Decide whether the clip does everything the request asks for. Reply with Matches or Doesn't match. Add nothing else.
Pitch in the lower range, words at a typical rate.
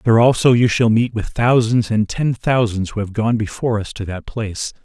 Doesn't match